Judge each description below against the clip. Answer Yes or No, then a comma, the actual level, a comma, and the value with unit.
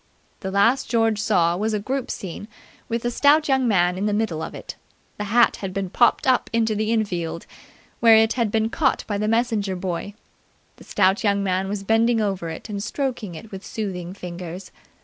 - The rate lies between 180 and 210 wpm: Yes, average, 200 wpm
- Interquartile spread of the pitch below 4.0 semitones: Yes, average, 3.3 semitones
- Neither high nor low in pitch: No, high, 210 Hz